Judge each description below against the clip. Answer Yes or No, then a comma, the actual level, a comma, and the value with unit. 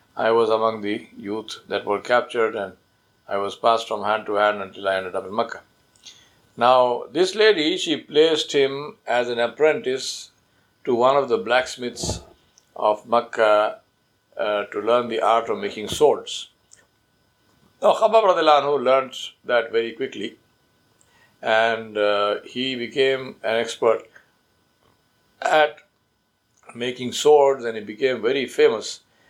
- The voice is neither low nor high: No, low, 120 Hz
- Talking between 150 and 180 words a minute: No, slow, 135 wpm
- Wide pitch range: No, average, 4.3 semitones